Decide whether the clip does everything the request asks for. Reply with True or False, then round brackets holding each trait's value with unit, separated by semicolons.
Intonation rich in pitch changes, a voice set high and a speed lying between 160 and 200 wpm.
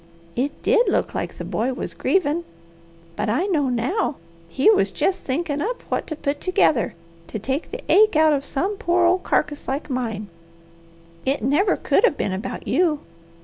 True (5.9 semitones; 295 Hz; 180 wpm)